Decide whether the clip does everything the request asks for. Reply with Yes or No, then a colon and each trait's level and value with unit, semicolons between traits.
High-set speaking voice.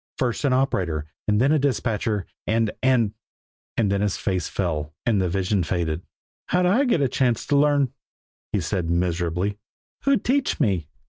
No: low, 105 Hz